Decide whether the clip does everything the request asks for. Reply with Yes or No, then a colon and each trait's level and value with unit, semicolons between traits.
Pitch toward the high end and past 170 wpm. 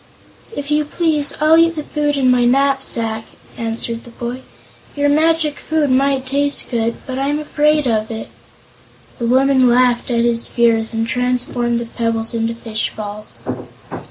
No: very high, 250 Hz; average, 155 wpm